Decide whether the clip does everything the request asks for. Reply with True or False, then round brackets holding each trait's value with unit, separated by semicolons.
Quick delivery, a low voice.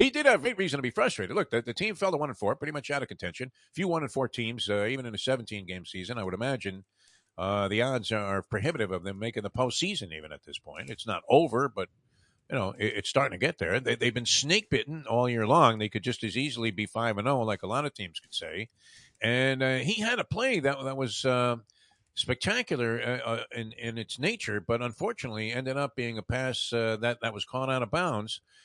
True (250 wpm; 120 Hz)